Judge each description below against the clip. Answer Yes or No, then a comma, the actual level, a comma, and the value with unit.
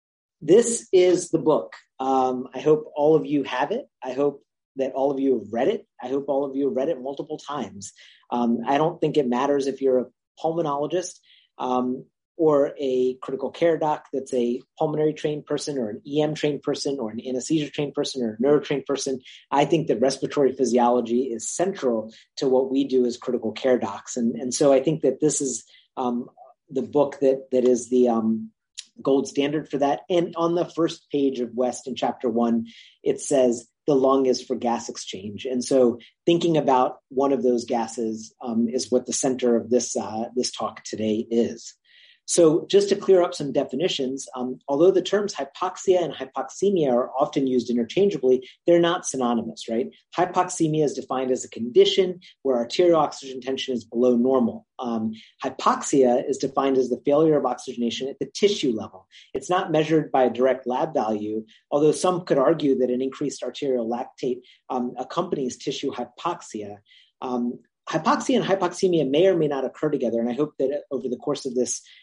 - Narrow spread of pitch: No, average, 3.6 semitones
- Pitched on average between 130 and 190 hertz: Yes, low, 135 Hz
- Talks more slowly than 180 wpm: No, average, 190 wpm